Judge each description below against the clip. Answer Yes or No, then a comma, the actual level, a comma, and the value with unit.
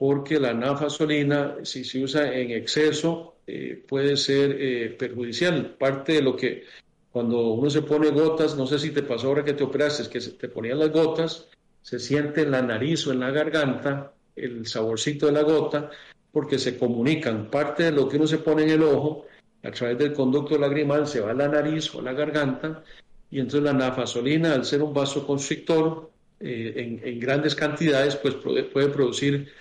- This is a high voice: No, medium, 145 Hz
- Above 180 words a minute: Yes, fast, 190 wpm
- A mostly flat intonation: Yes, narrow, 2.3 semitones